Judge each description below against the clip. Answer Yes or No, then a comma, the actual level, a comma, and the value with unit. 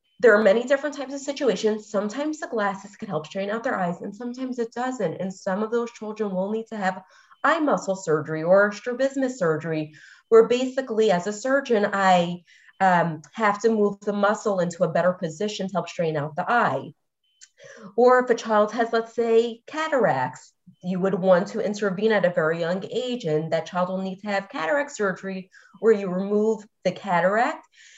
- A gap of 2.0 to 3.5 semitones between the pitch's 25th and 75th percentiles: No, average, 4.1 semitones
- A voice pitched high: Yes, high, 205 Hz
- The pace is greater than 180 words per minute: Yes, average, 190 wpm